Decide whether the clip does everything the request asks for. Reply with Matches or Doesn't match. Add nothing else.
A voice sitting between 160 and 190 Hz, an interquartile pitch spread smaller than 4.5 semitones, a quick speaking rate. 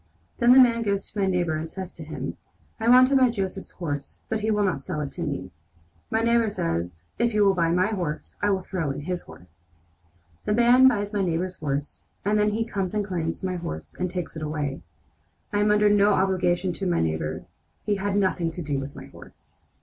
Doesn't match